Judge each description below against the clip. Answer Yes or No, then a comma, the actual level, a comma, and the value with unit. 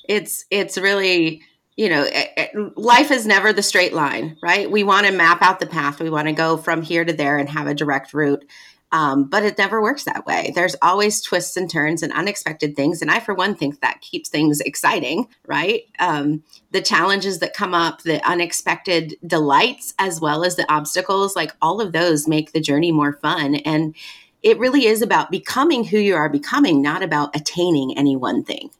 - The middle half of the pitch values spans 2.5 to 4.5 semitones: No, average, 5.2 semitones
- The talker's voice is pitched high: No, medium, 175 Hz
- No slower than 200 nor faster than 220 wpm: Yes, fast, 205 wpm